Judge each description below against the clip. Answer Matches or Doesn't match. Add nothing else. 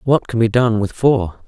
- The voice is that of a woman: Doesn't match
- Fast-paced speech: Matches